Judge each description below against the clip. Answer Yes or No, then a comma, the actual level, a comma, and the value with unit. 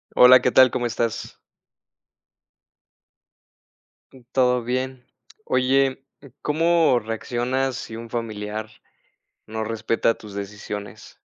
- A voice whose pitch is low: Yes, low, 120 Hz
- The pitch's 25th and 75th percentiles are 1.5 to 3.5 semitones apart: Yes, average, 2.8 semitones